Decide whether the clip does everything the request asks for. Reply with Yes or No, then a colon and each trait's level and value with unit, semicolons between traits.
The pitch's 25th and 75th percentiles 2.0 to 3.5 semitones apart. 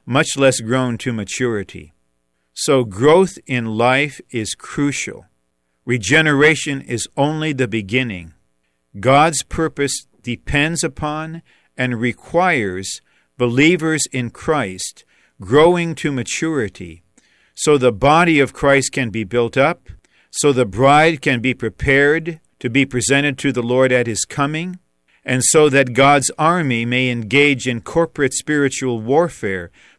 No: average, 4.0 semitones